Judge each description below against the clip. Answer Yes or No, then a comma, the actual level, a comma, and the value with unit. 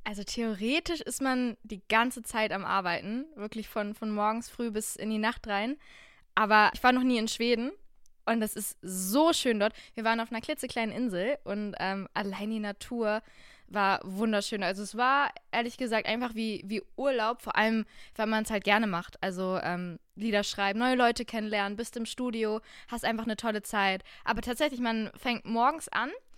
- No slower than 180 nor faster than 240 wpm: Yes, fast, 190 wpm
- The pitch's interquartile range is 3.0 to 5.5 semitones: No, narrow, 2.6 semitones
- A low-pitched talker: No, high, 220 Hz